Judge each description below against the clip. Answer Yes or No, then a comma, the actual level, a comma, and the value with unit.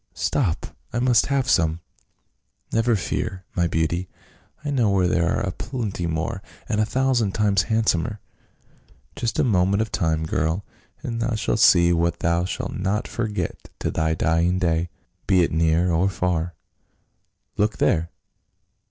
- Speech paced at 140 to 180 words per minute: Yes, average, 160 wpm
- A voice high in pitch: No, very low, 90 Hz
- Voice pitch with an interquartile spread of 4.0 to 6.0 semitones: Yes, average, 4.5 semitones